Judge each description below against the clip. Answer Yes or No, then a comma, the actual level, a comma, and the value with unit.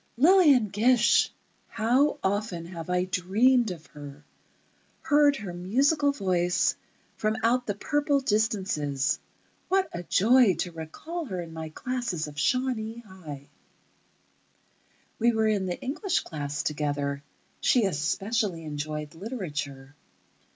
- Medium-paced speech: No, slow, 115 wpm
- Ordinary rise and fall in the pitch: No, wide, 7.7 semitones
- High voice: Yes, high, 195 Hz